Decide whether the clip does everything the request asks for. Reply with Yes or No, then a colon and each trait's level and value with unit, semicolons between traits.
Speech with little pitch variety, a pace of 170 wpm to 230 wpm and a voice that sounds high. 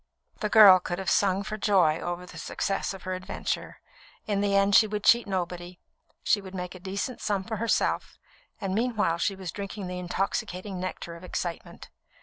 Yes: narrow, 2.1 semitones; average, 185 wpm; high, 195 Hz